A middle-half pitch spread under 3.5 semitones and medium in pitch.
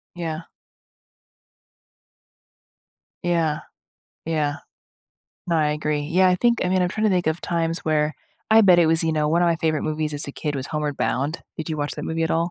Yes: narrow, 2.4 semitones; medium, 160 Hz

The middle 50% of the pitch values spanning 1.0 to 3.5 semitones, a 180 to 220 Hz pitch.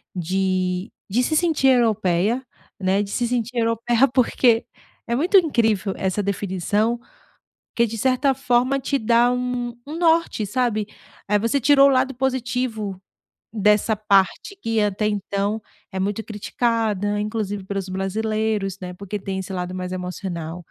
No: average, 4.2 semitones; high, 215 Hz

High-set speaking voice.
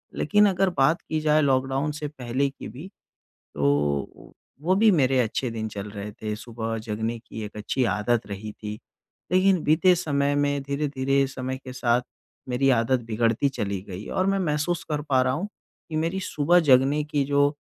No: low, 135 Hz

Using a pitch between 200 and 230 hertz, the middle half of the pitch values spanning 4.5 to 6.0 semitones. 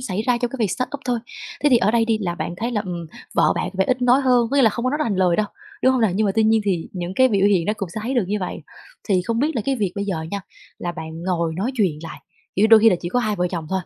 Yes: high, 210 Hz; average, 4.8 semitones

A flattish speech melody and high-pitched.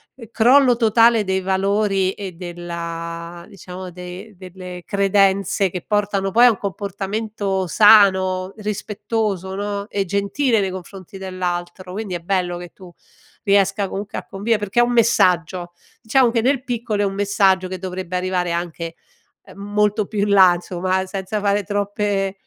Yes: narrow, 2.1 semitones; high, 195 Hz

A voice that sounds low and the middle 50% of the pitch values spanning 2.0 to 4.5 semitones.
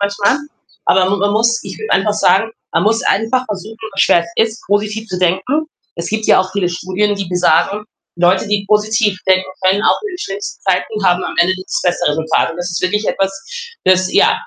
No: high, 200 Hz; average, 2.7 semitones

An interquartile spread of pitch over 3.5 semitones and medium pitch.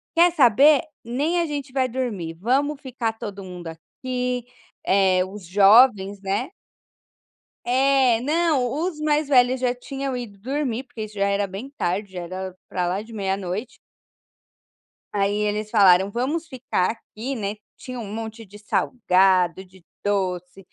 No: average, 5.1 semitones; high, 220 Hz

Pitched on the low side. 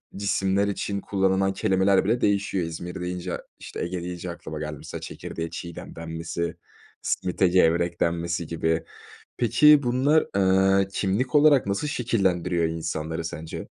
Yes: very low, 95 Hz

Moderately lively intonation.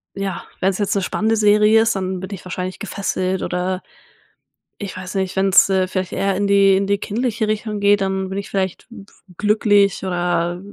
No: narrow, 1.7 semitones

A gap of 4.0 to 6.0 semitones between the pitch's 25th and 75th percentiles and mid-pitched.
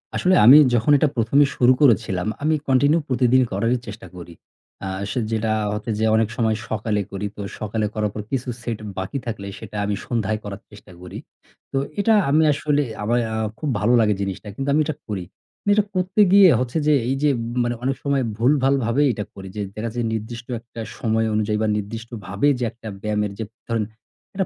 No: average, 4.3 semitones; low, 115 Hz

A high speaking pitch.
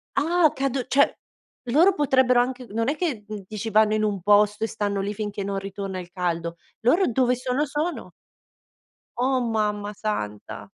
Yes: high, 215 Hz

